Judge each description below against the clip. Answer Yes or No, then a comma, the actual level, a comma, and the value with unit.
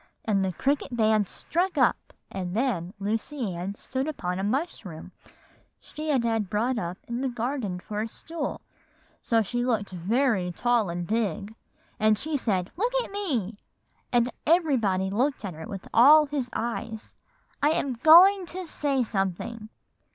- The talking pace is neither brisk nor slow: Yes, average, 160 wpm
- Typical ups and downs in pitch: No, wide, 5.9 semitones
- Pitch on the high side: Yes, high, 230 Hz